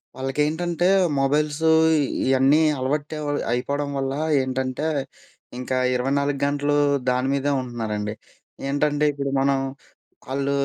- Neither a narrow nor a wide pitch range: No, narrow, 1.9 semitones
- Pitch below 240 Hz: Yes, medium, 140 Hz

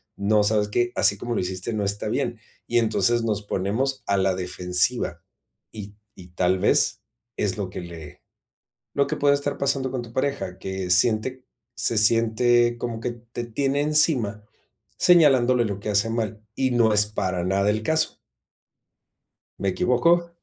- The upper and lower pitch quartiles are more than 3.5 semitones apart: Yes, average, 4.1 semitones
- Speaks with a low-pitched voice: Yes, low, 110 Hz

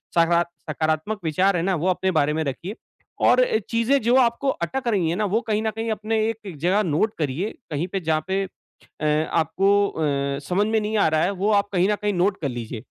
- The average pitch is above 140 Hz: Yes, high, 190 Hz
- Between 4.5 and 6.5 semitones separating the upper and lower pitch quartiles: Yes, average, 5.1 semitones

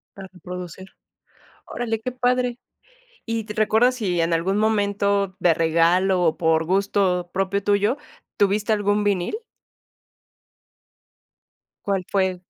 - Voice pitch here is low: No, high, 200 Hz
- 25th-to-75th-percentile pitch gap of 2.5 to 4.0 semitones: Yes, average, 3.0 semitones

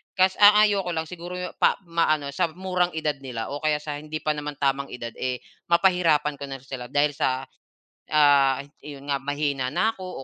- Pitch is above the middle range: No, medium, 150 Hz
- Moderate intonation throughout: Yes, average, 3.7 semitones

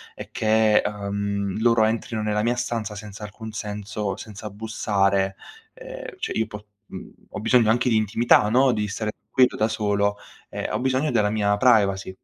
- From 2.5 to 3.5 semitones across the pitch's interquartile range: No, narrow, 2.1 semitones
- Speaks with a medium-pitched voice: No, low, 110 Hz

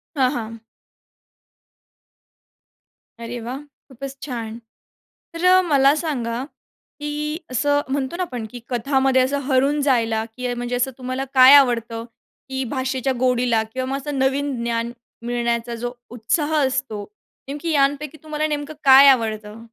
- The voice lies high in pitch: Yes, very high, 260 Hz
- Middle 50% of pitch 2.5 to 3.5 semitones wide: Yes, average, 3.0 semitones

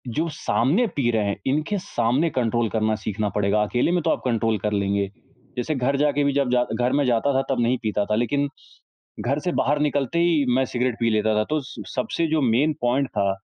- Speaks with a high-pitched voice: No, low, 125 Hz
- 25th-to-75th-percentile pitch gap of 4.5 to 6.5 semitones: Yes, average, 4.8 semitones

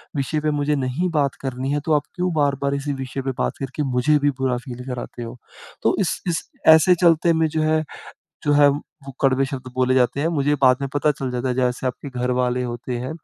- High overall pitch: No, low, 135 Hz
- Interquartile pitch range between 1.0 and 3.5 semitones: Yes, average, 2.8 semitones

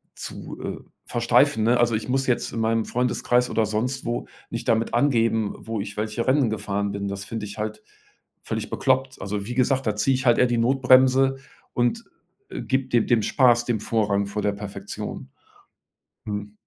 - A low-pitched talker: Yes, low, 115 Hz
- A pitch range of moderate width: Yes, average, 3.1 semitones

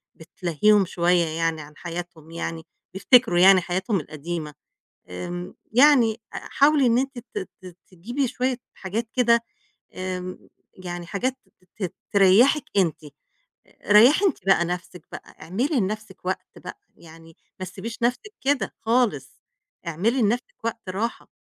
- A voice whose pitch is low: No, high, 190 Hz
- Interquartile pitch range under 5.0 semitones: No, wide, 5.5 semitones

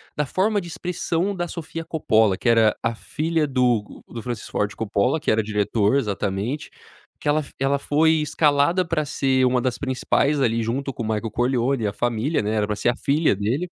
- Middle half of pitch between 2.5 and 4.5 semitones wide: No, wide, 5.5 semitones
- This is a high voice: No, low, 130 Hz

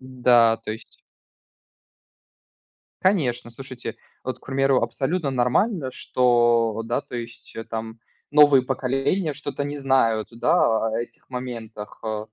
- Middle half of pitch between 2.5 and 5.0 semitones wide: Yes, average, 2.9 semitones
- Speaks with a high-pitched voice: No, low, 125 Hz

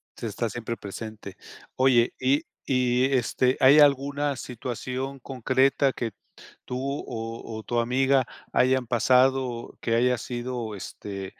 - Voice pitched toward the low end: Yes, low, 125 Hz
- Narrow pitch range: Yes, narrow, 2.3 semitones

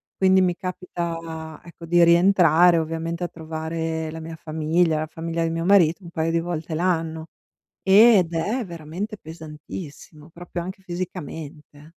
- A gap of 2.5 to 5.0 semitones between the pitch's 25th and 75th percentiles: No, narrow, 1.8 semitones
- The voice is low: No, medium, 165 Hz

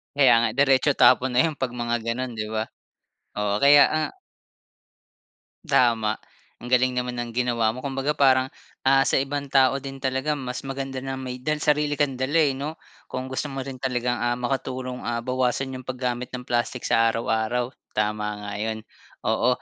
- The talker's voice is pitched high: No, low, 130 Hz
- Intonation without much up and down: Yes, narrow, 2.0 semitones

